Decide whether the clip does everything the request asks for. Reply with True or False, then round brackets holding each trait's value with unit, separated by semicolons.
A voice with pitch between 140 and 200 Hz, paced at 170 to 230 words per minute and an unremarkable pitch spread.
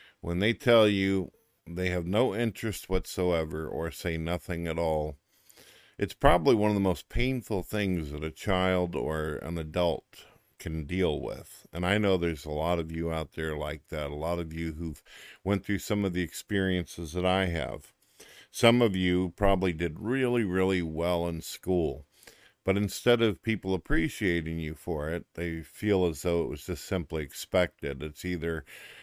False (90 Hz; 180 wpm; 3.1 semitones)